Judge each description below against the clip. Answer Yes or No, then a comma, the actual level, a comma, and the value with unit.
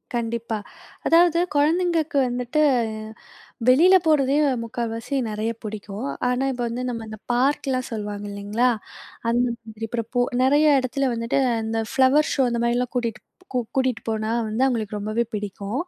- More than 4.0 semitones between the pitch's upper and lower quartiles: No, average, 3.4 semitones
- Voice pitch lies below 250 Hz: Yes, high, 240 Hz